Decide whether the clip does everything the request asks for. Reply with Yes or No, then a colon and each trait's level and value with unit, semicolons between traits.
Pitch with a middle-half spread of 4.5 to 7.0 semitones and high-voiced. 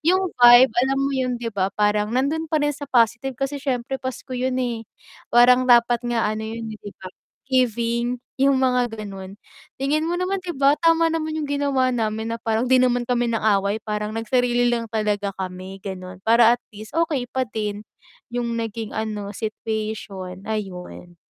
No: average, 3.5 semitones; high, 235 Hz